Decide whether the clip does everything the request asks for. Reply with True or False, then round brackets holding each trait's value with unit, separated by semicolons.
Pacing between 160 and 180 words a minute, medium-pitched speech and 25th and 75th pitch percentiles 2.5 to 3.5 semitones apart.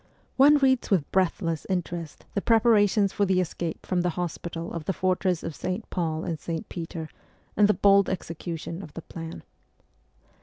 True (165 wpm; 180 Hz; 3.1 semitones)